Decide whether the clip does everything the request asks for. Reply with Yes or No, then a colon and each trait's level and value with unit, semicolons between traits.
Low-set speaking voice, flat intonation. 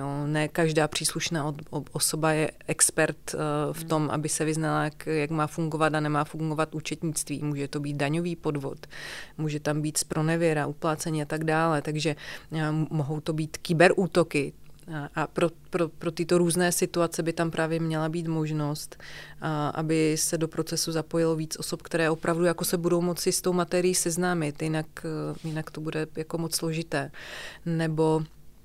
No: medium, 160 Hz; narrow, 1.5 semitones